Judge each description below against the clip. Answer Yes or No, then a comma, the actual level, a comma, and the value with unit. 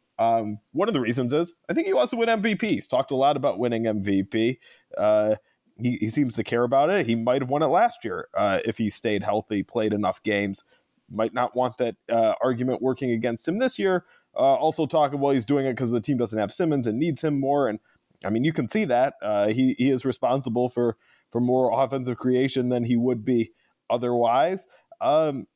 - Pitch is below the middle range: Yes, low, 125 Hz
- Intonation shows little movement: No, average, 3.7 semitones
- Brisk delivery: Yes, fast, 220 wpm